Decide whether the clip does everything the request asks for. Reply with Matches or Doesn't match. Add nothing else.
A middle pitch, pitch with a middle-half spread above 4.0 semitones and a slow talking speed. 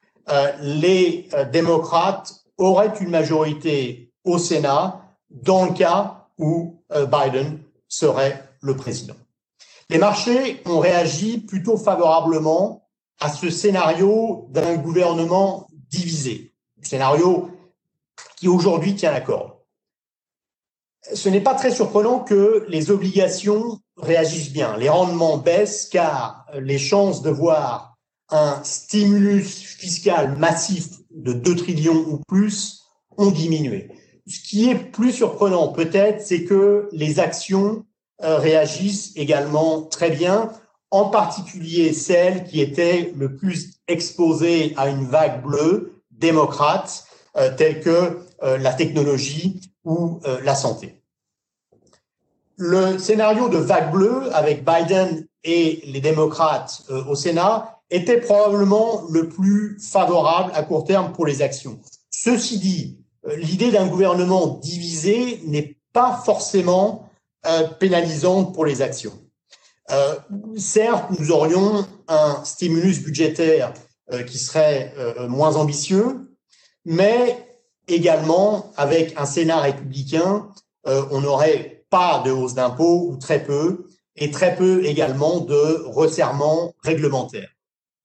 Matches